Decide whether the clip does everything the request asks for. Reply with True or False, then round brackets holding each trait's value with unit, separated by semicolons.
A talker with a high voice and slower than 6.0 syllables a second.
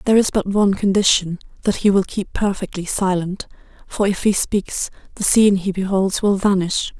True (195 Hz; 5.2 syllables/s)